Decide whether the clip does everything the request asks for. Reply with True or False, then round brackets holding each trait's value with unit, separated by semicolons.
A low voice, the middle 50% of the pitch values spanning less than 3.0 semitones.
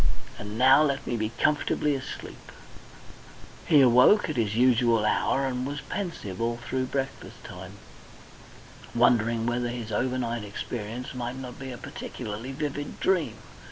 True (125 Hz; 2.6 semitones)